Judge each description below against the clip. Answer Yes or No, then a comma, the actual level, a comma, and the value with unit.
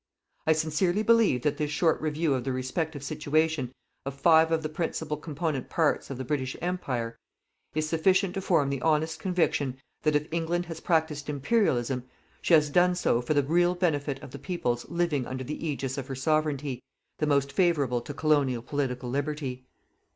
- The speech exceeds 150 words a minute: Yes, average, 180 wpm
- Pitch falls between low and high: Yes, medium, 150 Hz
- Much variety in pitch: No, average, 3.3 semitones